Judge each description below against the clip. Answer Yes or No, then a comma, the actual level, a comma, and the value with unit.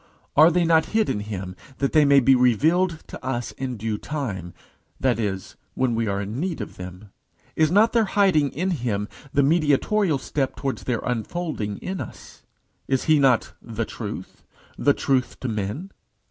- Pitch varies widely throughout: Yes, wide, 6.5 semitones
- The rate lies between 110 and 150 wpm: No, average, 175 wpm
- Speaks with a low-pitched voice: Yes, low, 130 Hz